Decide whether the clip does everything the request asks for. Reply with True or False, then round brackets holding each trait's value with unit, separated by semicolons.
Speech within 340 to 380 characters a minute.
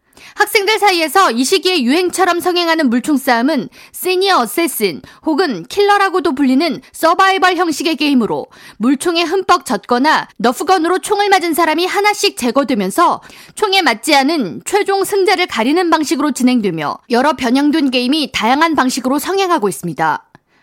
True (360 characters per minute)